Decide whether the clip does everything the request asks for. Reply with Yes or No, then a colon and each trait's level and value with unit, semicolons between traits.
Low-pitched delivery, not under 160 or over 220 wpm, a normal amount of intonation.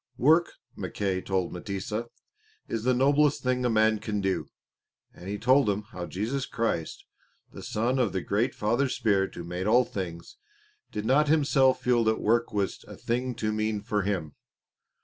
Yes: low, 110 Hz; average, 170 wpm; average, 4.3 semitones